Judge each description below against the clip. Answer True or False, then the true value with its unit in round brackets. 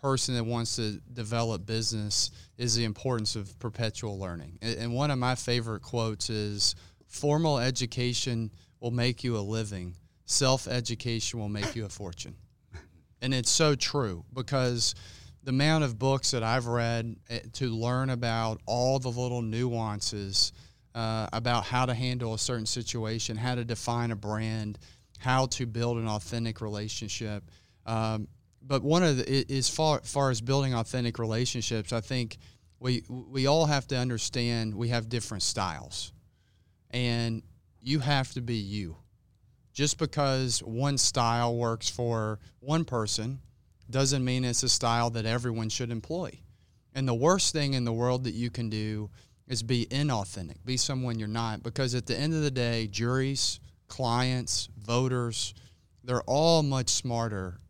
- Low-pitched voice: True (115 Hz)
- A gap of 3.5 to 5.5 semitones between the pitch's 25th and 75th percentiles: False (2.7 semitones)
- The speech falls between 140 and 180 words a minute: True (155 wpm)